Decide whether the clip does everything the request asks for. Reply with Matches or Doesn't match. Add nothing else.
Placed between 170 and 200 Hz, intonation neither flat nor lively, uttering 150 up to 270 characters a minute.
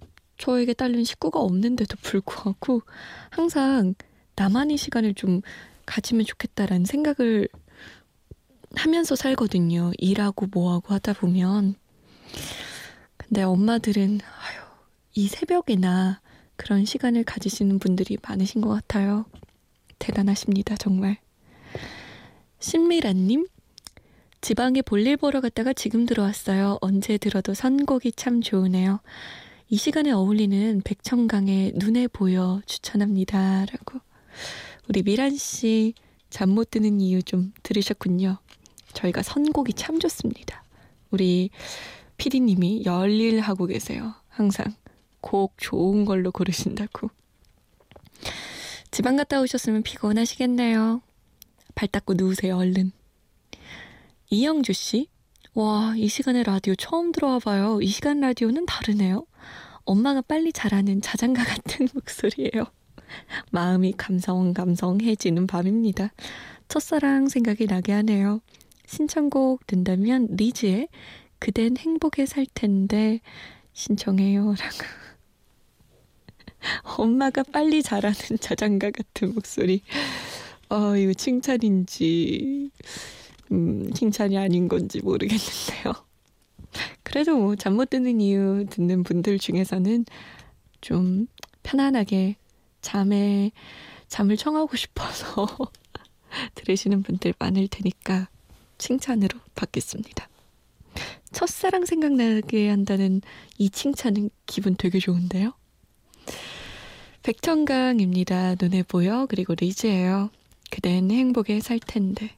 Doesn't match